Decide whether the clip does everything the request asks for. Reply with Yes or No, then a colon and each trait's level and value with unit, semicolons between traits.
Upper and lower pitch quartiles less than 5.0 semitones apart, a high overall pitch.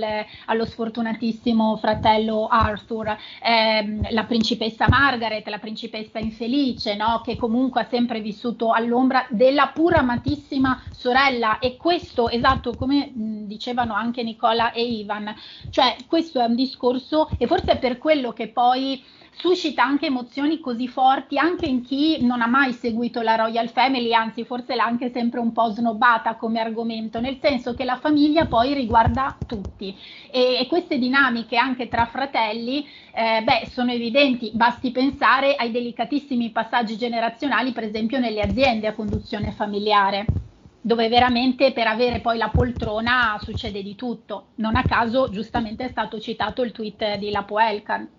Yes: narrow, 2.5 semitones; high, 240 Hz